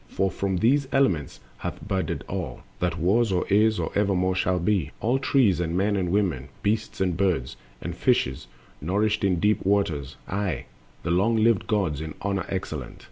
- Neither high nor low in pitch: No, very low, 95 Hz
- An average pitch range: Yes, average, 3.3 semitones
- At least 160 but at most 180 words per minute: Yes, average, 175 wpm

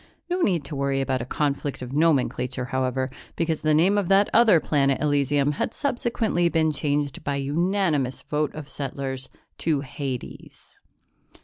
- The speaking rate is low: No, average, 150 wpm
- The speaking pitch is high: No, medium, 145 Hz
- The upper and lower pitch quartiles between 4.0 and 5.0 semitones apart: No, average, 3.5 semitones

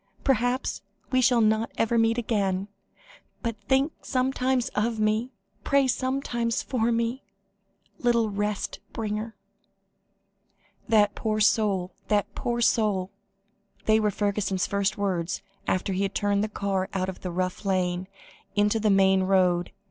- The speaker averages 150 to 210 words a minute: No, slow, 135 wpm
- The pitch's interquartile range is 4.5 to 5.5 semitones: No, average, 3.2 semitones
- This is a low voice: No, high, 215 Hz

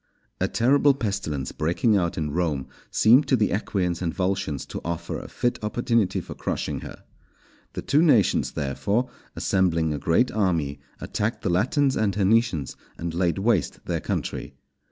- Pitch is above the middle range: No, very low, 95 Hz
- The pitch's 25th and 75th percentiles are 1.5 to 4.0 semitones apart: No, wide, 5.6 semitones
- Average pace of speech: Yes, average, 160 wpm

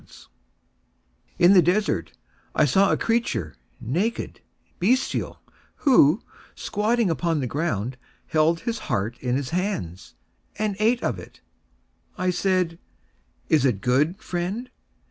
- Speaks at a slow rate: Yes, slow, 125 wpm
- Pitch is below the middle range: No, medium, 175 Hz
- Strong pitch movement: Yes, wide, 8.0 semitones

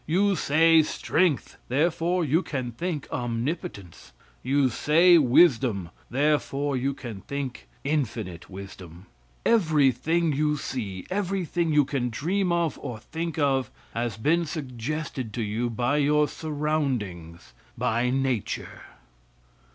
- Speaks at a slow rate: Yes, slow, 115 wpm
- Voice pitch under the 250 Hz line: Yes, medium, 140 Hz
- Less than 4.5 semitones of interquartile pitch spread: No, average, 4.9 semitones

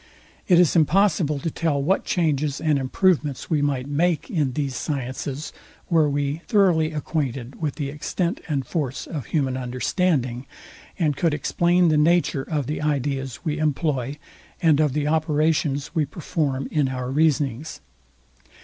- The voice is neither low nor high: Yes, medium, 150 Hz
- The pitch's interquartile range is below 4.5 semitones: Yes, average, 2.8 semitones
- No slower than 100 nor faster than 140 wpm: No, average, 150 wpm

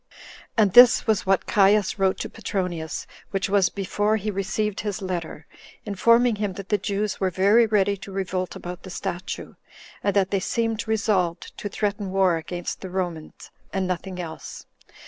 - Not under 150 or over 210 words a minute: Yes, average, 165 wpm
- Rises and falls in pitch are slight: Yes, narrow, 2.2 semitones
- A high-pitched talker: Yes, high, 195 Hz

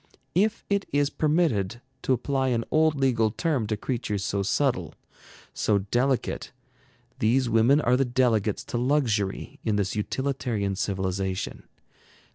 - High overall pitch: No, low, 120 Hz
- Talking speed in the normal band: No, slow, 130 wpm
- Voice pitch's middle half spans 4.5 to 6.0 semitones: Yes, average, 5.0 semitones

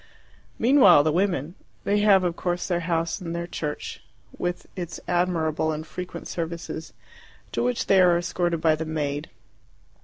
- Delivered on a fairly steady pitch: Yes, narrow, 2.3 semitones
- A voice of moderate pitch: Yes, medium, 170 Hz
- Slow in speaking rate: No, average, 155 wpm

